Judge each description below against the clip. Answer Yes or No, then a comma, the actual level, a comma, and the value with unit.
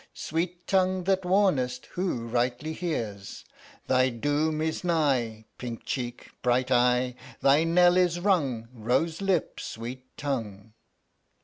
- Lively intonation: Yes, wide, 6.1 semitones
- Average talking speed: No, slow, 120 wpm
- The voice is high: No, medium, 140 Hz